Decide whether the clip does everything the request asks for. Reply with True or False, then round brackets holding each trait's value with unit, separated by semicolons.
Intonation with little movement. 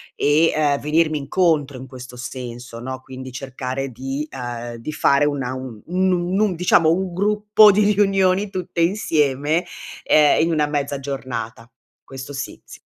False (5.1 semitones)